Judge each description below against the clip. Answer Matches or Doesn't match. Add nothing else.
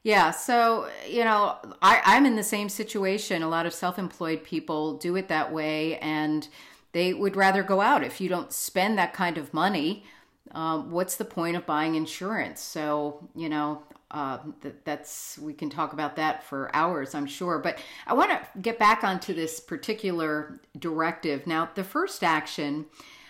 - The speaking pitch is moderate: Matches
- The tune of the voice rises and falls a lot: Doesn't match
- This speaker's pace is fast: Doesn't match